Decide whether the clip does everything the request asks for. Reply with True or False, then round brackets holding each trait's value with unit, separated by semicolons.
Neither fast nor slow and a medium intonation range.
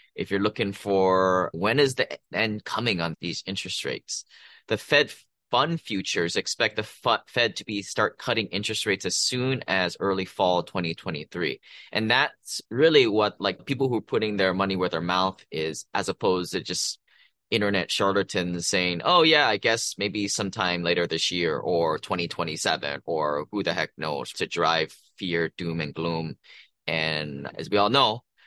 True (175 wpm; 3.6 semitones)